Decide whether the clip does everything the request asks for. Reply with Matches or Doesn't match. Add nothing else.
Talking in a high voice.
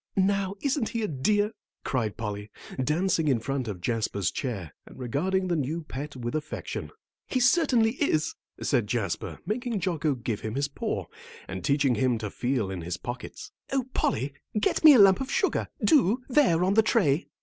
Doesn't match